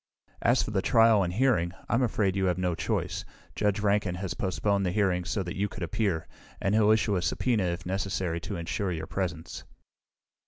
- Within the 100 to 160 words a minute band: No, average, 195 wpm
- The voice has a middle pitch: No, very low, 95 Hz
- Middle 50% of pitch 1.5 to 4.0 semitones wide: Yes, average, 2.9 semitones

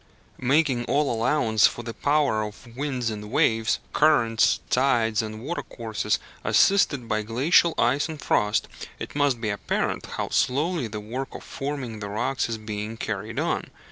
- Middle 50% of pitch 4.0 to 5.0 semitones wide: Yes, average, 4.5 semitones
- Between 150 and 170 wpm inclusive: Yes, average, 155 wpm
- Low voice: Yes, low, 120 Hz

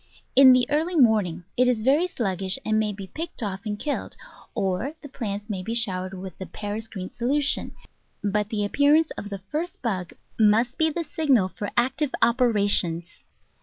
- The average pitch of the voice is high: Yes, high, 220 Hz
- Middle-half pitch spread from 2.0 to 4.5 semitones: No, wide, 5.4 semitones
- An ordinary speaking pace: Yes, average, 175 wpm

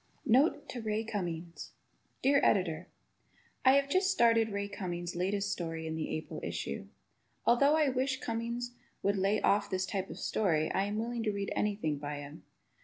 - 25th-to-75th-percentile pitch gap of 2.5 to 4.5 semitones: No, average, 5.3 semitones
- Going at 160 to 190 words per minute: Yes, average, 175 wpm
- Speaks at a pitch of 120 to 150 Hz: No, high, 205 Hz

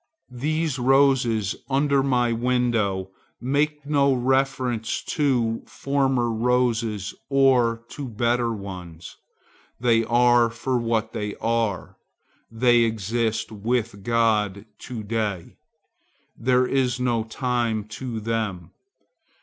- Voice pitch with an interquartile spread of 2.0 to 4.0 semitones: Yes, narrow, 2.5 semitones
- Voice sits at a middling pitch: No, low, 120 Hz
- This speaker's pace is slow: Yes, slow, 100 wpm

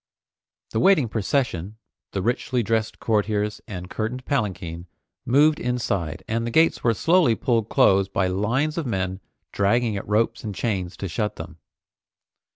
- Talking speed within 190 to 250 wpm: No, average, 150 wpm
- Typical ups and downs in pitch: Yes, average, 4.0 semitones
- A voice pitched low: Yes, low, 110 Hz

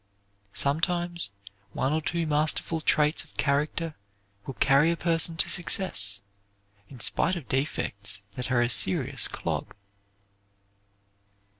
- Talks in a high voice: No, medium, 150 Hz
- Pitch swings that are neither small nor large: Yes, average, 4.8 semitones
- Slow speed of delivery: Yes, slow, 120 wpm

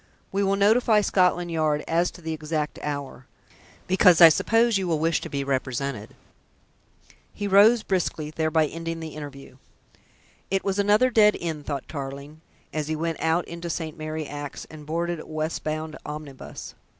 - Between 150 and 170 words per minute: Yes, average, 165 wpm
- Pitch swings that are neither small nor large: Yes, average, 3.2 semitones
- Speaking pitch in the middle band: Yes, medium, 160 Hz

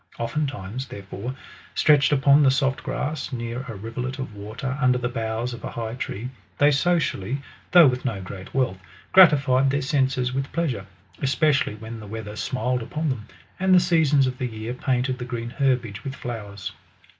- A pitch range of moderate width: Yes, average, 3.4 semitones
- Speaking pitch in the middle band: No, low, 130 Hz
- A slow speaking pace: No, average, 170 wpm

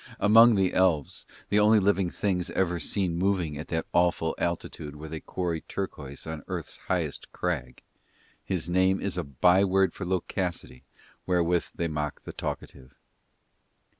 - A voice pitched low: Yes, very low, 90 Hz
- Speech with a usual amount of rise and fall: Yes, average, 3.0 semitones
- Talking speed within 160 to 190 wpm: No, average, 145 wpm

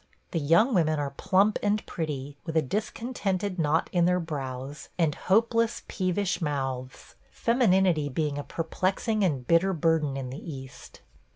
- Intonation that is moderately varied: Yes, average, 5.0 semitones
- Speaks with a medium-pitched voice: Yes, medium, 165 Hz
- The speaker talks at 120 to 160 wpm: Yes, average, 155 wpm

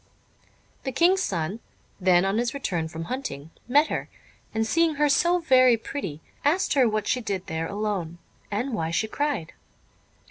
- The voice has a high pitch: Yes, high, 220 Hz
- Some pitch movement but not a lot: No, wide, 8.1 semitones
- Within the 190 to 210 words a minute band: No, average, 165 wpm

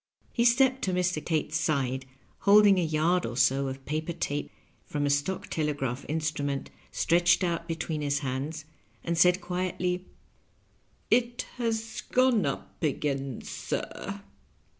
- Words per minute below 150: Yes, average, 140 wpm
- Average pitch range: Yes, average, 4.4 semitones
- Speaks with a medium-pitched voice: Yes, medium, 160 Hz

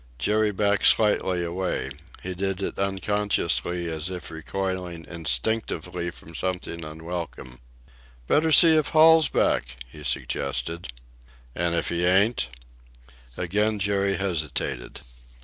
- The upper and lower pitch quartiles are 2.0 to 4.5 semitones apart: Yes, average, 3.7 semitones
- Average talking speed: No, slow, 115 wpm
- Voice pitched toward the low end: Yes, very low, 90 Hz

